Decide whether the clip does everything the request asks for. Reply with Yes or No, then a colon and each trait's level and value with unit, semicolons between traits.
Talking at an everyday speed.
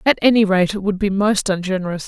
No: fast, 230 wpm